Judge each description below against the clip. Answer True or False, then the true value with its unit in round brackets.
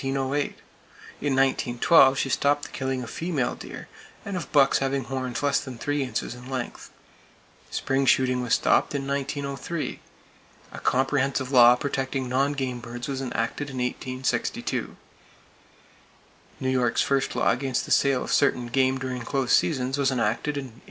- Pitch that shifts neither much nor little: False (1.7 semitones)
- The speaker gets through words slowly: False (155 wpm)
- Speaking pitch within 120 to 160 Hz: True (135 Hz)